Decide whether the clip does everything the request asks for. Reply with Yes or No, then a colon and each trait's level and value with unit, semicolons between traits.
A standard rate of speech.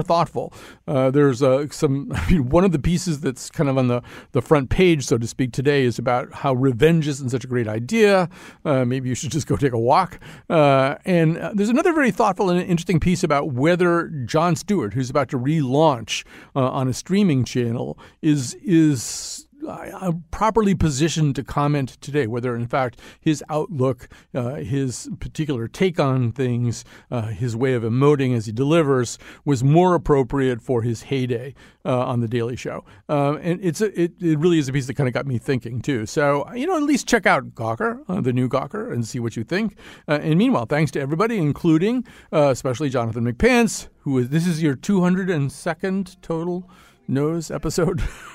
Yes: average, 190 wpm